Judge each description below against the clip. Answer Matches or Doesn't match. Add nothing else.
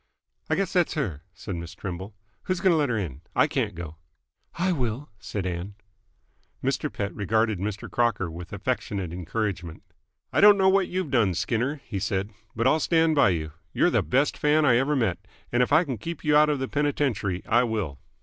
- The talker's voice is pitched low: Matches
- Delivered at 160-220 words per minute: Matches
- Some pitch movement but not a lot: Doesn't match